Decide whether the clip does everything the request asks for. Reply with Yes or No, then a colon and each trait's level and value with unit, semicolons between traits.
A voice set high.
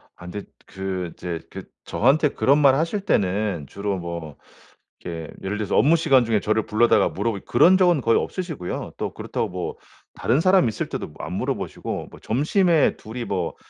No: low, 110 Hz